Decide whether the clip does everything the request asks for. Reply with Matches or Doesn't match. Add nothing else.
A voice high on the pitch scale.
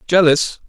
Doesn't match